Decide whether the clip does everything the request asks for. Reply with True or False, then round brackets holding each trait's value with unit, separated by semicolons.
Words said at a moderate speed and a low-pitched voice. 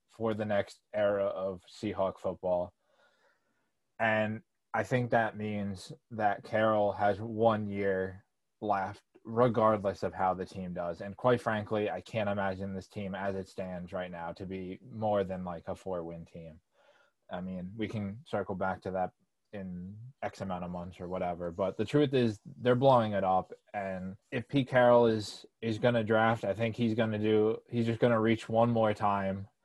True (180 wpm; 100 Hz)